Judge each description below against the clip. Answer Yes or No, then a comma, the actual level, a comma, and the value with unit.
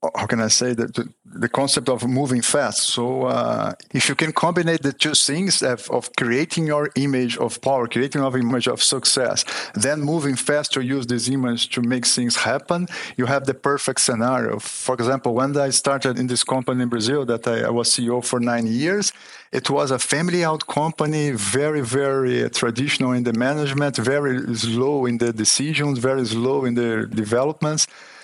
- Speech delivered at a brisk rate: No, average, 185 wpm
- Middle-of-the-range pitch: No, low, 130 Hz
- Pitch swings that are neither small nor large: Yes, average, 3.0 semitones